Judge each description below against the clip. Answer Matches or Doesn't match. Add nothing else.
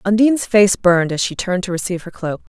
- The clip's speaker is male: Doesn't match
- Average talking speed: Doesn't match